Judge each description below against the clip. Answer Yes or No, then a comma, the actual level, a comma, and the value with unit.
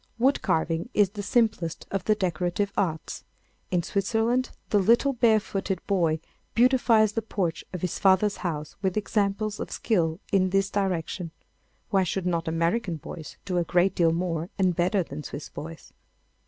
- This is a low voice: No, high, 190 Hz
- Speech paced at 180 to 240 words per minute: No, average, 160 wpm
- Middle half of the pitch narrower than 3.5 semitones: No, average, 3.8 semitones